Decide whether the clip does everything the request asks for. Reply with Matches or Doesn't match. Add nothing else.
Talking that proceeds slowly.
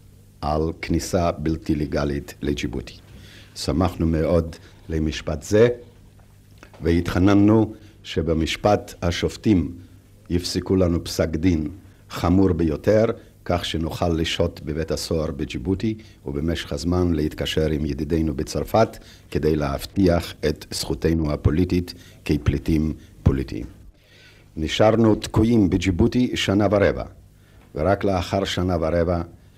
Matches